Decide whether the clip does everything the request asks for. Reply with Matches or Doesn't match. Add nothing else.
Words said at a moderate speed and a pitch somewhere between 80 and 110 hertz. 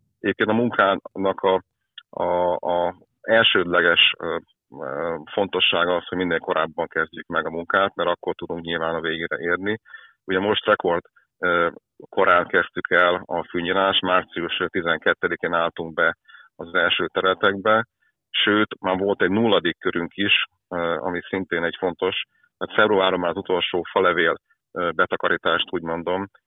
Matches